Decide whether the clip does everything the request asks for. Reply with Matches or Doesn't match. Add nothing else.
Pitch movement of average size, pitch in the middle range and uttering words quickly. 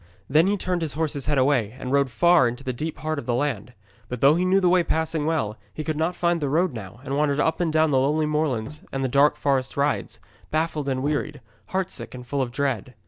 Matches